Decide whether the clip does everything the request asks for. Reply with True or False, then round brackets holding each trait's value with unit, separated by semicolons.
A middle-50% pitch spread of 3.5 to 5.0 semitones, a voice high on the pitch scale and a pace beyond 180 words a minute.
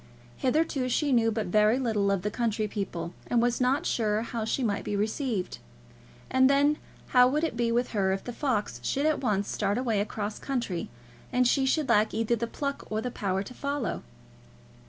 True (3.9 semitones; 230 Hz; 200 wpm)